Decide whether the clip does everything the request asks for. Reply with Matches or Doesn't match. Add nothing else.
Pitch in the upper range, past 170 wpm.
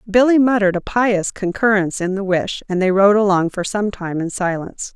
Matches